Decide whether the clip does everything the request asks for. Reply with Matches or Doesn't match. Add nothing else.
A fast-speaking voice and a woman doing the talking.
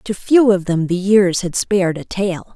Matches